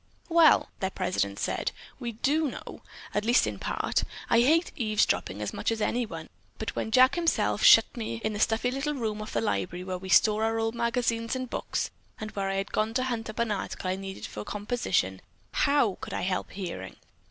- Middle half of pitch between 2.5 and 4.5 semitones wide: Yes, average, 4.2 semitones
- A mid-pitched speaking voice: No, high, 220 Hz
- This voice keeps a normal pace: No, fast, 210 wpm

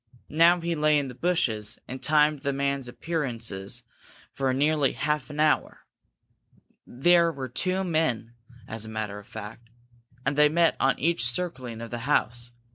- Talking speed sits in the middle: Yes, average, 160 wpm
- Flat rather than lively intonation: No, average, 4.7 semitones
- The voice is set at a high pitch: No, medium, 140 Hz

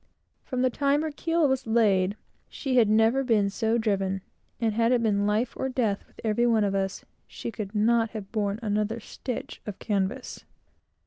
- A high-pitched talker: Yes, high, 225 Hz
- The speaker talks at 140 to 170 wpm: No, average, 185 wpm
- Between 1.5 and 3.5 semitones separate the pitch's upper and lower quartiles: Yes, average, 3.1 semitones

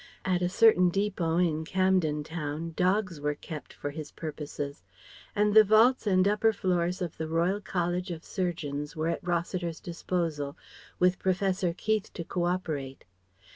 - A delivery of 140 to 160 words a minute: Yes, average, 155 wpm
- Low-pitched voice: No, medium, 175 Hz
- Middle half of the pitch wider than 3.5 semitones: No, average, 3.0 semitones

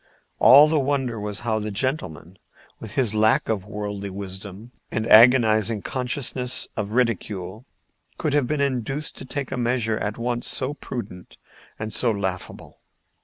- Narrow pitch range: No, average, 3.9 semitones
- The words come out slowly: No, average, 150 wpm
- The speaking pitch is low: Yes, low, 115 Hz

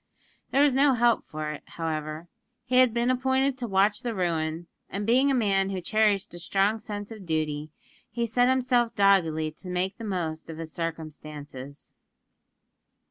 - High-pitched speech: Yes, high, 195 Hz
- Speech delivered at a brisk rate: No, average, 170 wpm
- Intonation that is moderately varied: No, wide, 6.8 semitones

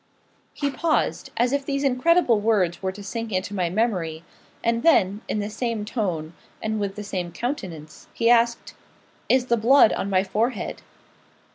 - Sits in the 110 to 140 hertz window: No, high, 220 Hz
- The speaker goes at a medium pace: Yes, average, 165 wpm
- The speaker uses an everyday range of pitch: Yes, average, 4.3 semitones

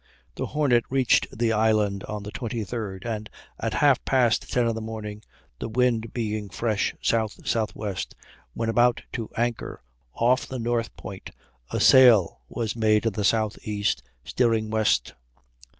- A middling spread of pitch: No, narrow, 2.0 semitones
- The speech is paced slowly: No, average, 145 wpm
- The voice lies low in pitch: Yes, low, 110 Hz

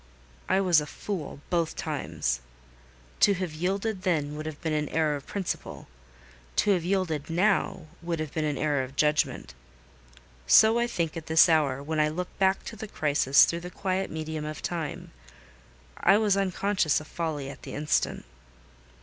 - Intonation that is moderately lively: Yes, average, 3.9 semitones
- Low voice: No, medium, 160 Hz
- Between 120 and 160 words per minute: No, average, 175 wpm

